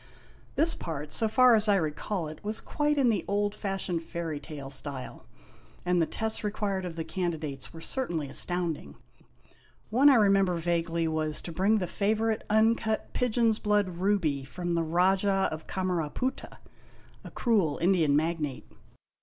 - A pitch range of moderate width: Yes, average, 4.8 semitones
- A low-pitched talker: No, medium, 180 Hz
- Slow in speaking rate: No, average, 155 wpm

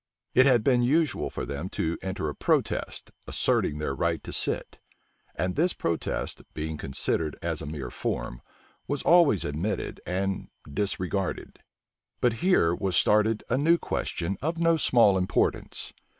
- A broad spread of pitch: Yes, wide, 8.2 semitones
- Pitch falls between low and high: No, very low, 95 Hz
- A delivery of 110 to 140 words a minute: No, average, 150 wpm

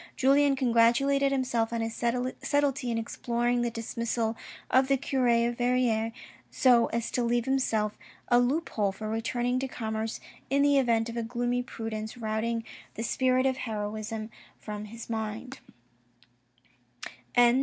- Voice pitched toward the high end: Yes, high, 235 Hz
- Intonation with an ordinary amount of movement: No, narrow, 2.3 semitones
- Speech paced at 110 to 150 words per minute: Yes, average, 145 wpm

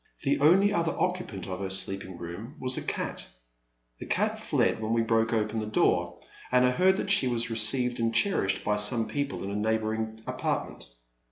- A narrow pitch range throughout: No, average, 4.0 semitones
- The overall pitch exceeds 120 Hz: No, low, 115 Hz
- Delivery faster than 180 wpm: Yes, average, 195 wpm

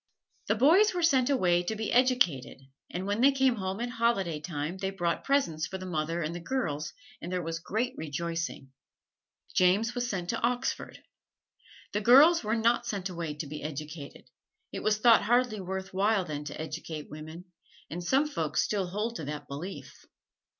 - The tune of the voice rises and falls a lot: Yes, wide, 6.5 semitones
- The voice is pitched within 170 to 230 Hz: Yes, high, 190 Hz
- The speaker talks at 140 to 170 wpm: No, average, 180 wpm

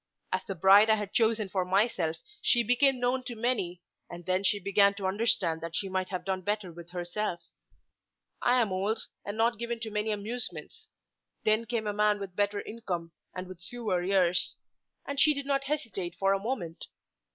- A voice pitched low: No, high, 205 Hz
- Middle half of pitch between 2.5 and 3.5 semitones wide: No, average, 3.9 semitones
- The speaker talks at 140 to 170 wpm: No, average, 195 wpm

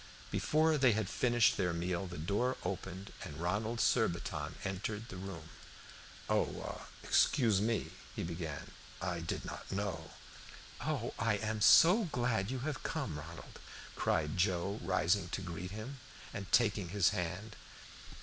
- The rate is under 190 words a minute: Yes, average, 140 wpm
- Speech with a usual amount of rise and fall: Yes, average, 4.7 semitones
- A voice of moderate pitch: No, low, 100 Hz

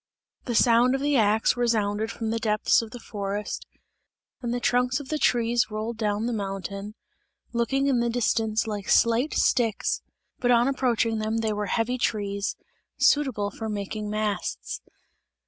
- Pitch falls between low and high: No, high, 225 Hz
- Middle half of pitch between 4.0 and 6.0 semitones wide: No, narrow, 2.5 semitones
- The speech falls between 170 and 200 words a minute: No, average, 160 wpm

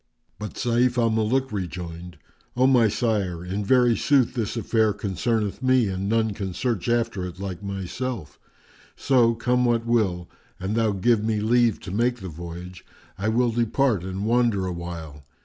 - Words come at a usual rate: Yes, average, 165 wpm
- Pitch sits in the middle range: No, low, 110 Hz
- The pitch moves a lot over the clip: No, average, 4.3 semitones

